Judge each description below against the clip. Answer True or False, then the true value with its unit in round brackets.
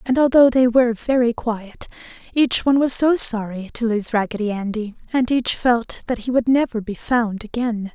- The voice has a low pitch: False (235 Hz)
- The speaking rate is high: False (190 wpm)